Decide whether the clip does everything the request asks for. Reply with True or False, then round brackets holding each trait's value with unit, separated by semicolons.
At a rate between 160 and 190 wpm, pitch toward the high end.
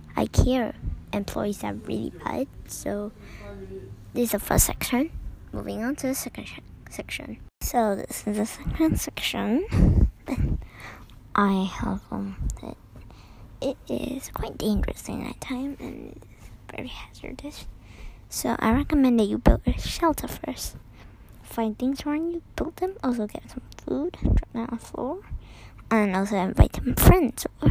False (150 wpm; 220 Hz)